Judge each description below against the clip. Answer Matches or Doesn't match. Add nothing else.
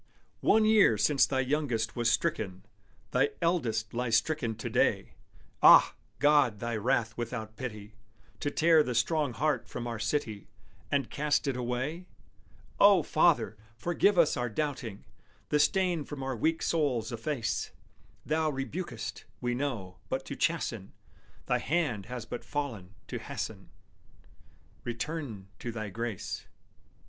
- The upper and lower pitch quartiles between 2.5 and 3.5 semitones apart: Doesn't match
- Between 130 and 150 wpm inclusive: Matches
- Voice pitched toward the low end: Matches